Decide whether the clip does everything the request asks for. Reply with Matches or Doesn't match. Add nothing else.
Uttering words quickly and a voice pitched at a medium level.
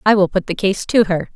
Doesn't match